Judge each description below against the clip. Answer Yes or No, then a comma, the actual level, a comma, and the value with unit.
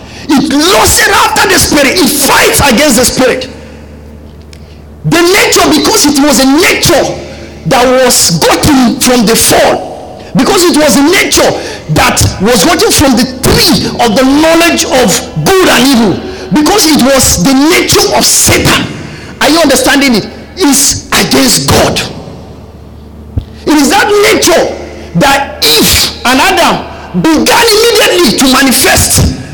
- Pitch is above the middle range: Yes, very high, 280 Hz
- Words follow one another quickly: No, average, 140 wpm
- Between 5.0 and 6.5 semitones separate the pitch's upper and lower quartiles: Yes, wide, 5.4 semitones